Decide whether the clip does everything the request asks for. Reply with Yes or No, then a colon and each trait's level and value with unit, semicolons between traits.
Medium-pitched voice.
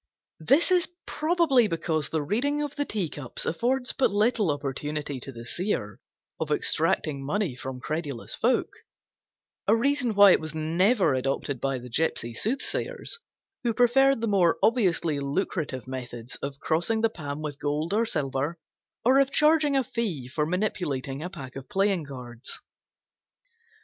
Yes: medium, 165 Hz